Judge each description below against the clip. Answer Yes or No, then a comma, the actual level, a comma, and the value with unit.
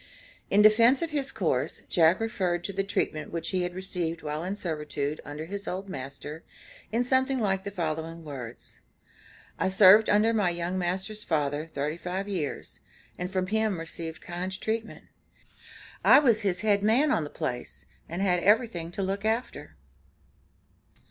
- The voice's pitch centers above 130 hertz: Yes, medium, 185 Hz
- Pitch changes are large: No, average, 4.4 semitones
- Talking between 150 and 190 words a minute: Yes, average, 160 wpm